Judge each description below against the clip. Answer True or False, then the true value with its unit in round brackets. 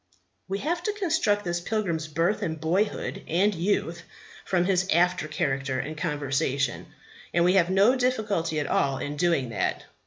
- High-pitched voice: False (175 Hz)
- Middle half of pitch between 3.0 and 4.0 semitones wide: False (4.9 semitones)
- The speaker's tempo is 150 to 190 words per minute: True (160 wpm)